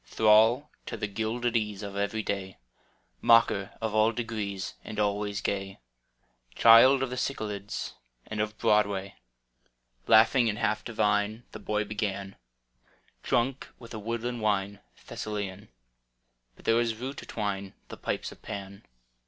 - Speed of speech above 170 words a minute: No, average, 145 wpm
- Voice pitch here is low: Yes, low, 105 Hz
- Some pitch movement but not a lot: No, narrow, 2.2 semitones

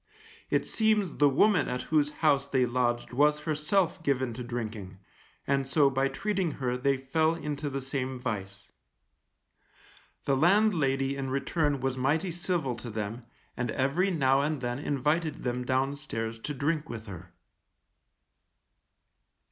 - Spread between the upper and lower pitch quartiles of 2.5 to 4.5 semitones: Yes, average, 3.4 semitones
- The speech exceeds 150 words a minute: No, average, 140 wpm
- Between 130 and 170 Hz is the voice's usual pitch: Yes, low, 135 Hz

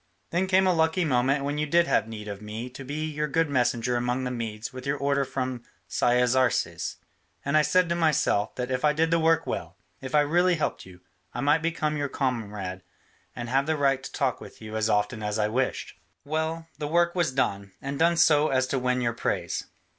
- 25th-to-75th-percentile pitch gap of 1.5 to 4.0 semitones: No, average, 4.6 semitones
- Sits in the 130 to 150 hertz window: Yes, low, 135 Hz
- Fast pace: Yes, fast, 220 wpm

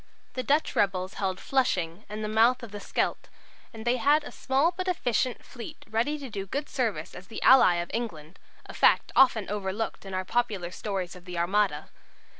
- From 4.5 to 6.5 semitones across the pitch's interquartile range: Yes, average, 5.1 semitones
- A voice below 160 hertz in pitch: No, high, 215 Hz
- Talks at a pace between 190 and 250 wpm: Yes, average, 195 wpm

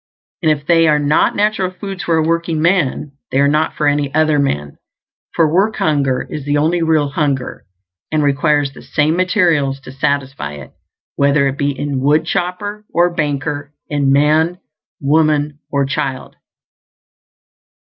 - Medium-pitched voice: Yes, medium, 150 Hz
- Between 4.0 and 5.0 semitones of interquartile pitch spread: No, average, 2.7 semitones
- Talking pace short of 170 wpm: Yes, average, 150 wpm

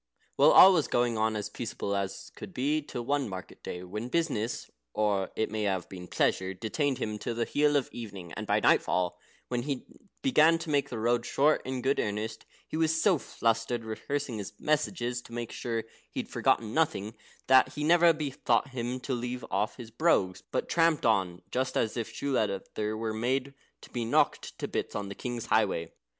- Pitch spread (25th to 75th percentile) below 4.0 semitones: No, average, 4.9 semitones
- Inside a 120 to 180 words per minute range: No, average, 195 wpm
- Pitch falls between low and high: No, low, 120 Hz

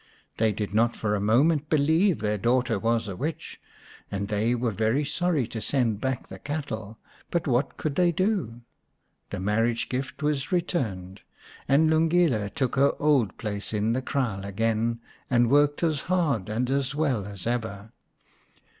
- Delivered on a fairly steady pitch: No, average, 5.3 semitones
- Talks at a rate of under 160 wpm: No, average, 165 wpm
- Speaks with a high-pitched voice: No, low, 120 Hz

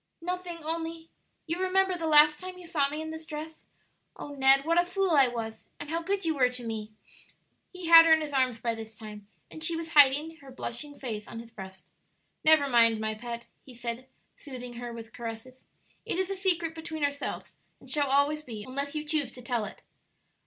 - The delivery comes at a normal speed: No, fast, 210 wpm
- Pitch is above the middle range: Yes, very high, 285 Hz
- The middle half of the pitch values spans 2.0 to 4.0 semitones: No, wide, 5.4 semitones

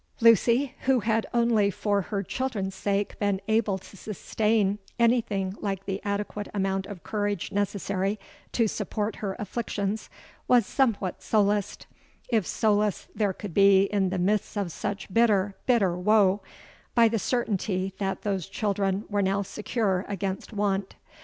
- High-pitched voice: Yes, high, 205 Hz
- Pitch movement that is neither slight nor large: No, narrow, 2.0 semitones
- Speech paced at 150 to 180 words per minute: No, average, 140 wpm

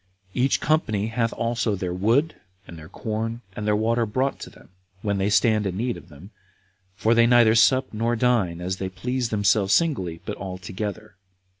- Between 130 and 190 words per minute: Yes, average, 180 wpm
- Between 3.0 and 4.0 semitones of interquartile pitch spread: Yes, average, 3.4 semitones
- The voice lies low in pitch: Yes, low, 110 Hz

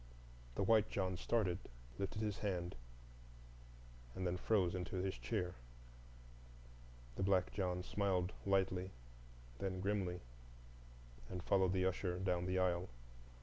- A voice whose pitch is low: Yes, very low, 95 Hz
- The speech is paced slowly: Yes, slow, 120 wpm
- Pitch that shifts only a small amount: Yes, narrow, 1.4 semitones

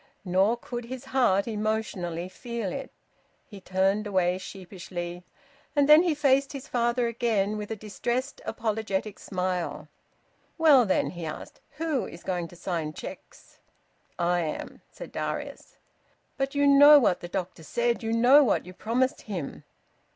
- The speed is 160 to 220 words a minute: No, average, 150 wpm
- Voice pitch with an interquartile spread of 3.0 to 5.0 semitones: No, wide, 5.6 semitones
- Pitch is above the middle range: Yes, high, 215 Hz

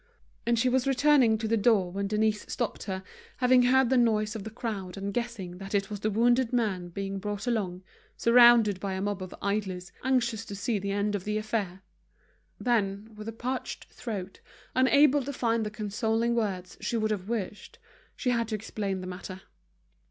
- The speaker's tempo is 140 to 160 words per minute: No, average, 190 wpm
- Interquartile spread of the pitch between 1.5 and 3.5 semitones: Yes, average, 3.2 semitones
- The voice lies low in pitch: No, high, 215 Hz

